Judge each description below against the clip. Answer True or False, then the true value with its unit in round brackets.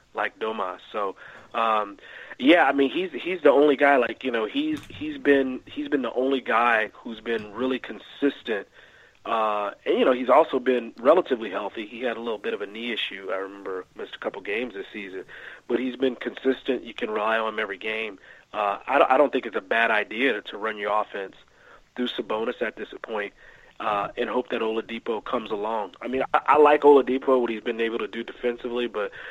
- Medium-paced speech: False (215 wpm)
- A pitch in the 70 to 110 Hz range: False (125 Hz)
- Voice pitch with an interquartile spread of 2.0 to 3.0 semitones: False (3.5 semitones)